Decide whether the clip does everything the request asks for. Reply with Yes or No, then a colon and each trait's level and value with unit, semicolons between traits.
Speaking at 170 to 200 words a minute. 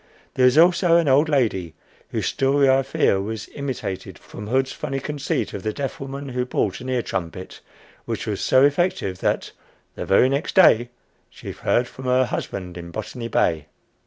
Yes: average, 180 wpm